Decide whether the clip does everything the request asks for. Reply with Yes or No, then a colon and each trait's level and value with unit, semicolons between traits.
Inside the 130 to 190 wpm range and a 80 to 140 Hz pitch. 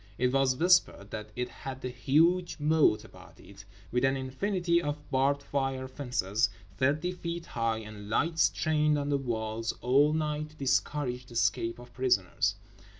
Yes: average, 160 wpm; low, 135 Hz